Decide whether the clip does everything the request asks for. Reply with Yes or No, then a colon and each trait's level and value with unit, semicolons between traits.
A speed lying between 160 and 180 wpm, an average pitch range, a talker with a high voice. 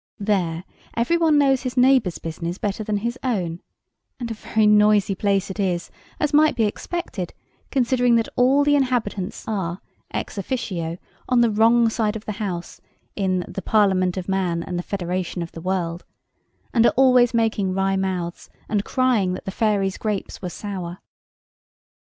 Yes: average, 170 wpm; average, 4.4 semitones; high, 205 Hz